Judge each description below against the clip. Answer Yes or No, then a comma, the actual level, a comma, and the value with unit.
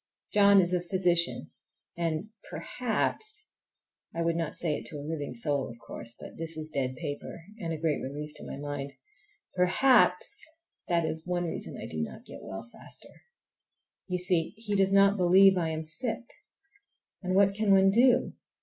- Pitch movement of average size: Yes, average, 4.4 semitones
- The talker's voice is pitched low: No, medium, 170 Hz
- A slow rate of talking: No, average, 165 wpm